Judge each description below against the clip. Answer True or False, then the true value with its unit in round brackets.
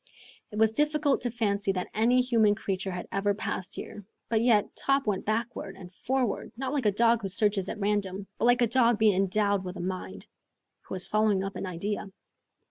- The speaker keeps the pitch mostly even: False (3.3 semitones)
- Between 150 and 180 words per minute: False (205 wpm)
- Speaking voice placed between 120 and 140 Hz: False (210 Hz)